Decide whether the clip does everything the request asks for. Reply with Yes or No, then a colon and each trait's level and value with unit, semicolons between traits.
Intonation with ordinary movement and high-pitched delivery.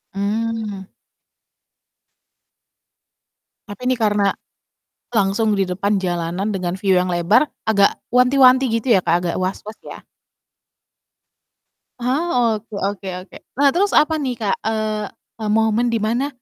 Yes: average, 3.5 semitones; high, 215 Hz